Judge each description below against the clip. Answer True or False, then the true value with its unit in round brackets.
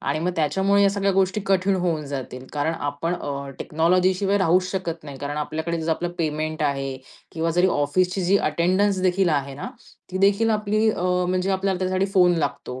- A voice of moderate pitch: True (175 Hz)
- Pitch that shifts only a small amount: False (4.1 semitones)